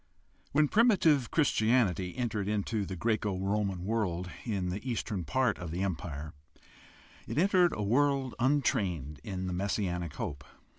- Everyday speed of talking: Yes, average, 155 wpm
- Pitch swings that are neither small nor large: No, wide, 6.0 semitones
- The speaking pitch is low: Yes, low, 105 Hz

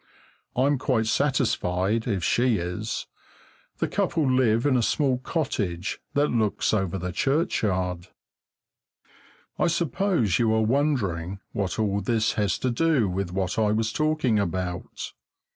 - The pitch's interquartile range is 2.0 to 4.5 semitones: No, wide, 5.5 semitones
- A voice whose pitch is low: Yes, low, 110 Hz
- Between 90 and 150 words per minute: Yes, slow, 135 wpm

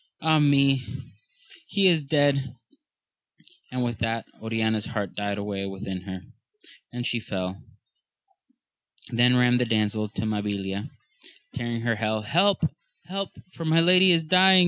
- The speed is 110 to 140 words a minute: Yes, slow, 135 wpm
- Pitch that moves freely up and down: Yes, wide, 6.1 semitones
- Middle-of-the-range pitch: No, low, 120 Hz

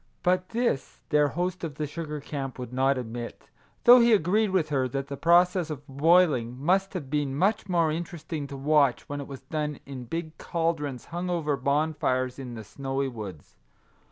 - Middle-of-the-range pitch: Yes, medium, 150 Hz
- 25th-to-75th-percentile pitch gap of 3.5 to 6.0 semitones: Yes, average, 4.2 semitones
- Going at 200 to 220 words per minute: No, average, 185 wpm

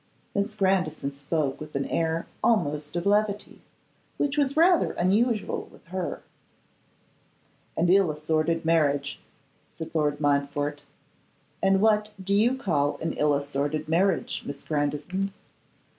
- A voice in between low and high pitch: Yes, medium, 165 Hz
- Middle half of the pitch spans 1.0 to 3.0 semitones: No, wide, 5.4 semitones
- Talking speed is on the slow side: Yes, slow, 125 wpm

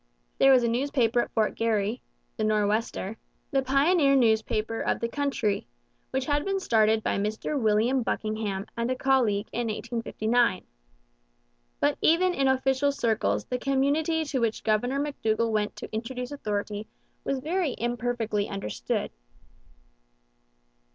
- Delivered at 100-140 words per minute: Yes, slow, 135 wpm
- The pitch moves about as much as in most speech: Yes, average, 3.9 semitones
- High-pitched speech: Yes, high, 235 Hz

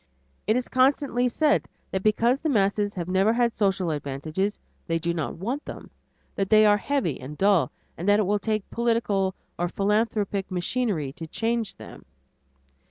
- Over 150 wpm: Yes, average, 165 wpm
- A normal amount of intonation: Yes, average, 4.3 semitones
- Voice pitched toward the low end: No, high, 205 Hz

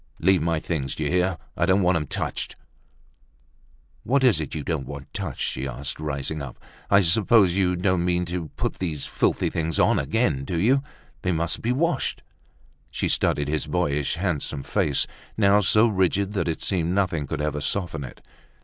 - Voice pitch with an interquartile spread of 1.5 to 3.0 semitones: No, average, 4.2 semitones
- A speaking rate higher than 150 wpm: Yes, average, 175 wpm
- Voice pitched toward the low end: Yes, very low, 85 Hz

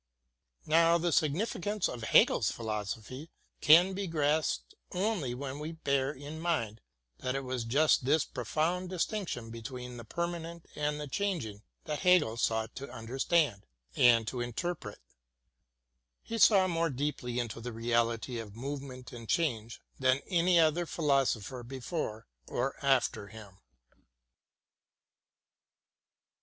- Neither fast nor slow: No, slow, 130 wpm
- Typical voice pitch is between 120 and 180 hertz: Yes, medium, 140 Hz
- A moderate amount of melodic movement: No, wide, 5.9 semitones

